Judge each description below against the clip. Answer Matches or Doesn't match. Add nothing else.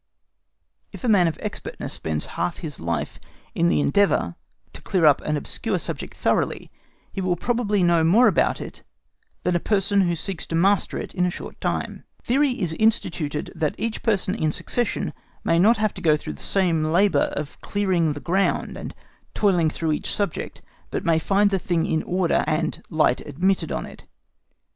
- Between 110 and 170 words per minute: Doesn't match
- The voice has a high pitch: Doesn't match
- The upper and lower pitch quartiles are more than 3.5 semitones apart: Matches